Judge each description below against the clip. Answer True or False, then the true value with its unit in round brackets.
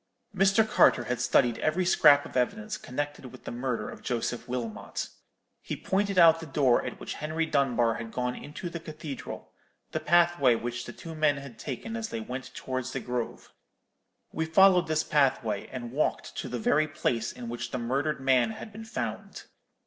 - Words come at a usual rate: True (185 wpm)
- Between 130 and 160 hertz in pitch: True (135 Hz)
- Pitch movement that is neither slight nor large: True (4.8 semitones)